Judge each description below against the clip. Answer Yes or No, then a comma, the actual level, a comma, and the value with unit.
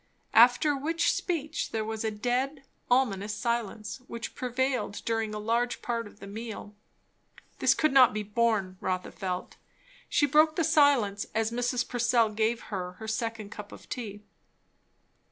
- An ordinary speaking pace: Yes, average, 155 wpm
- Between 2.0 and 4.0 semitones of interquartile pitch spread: Yes, average, 3.2 semitones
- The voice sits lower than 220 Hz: No, high, 230 Hz